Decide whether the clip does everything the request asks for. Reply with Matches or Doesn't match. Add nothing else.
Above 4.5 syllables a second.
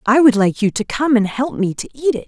Matches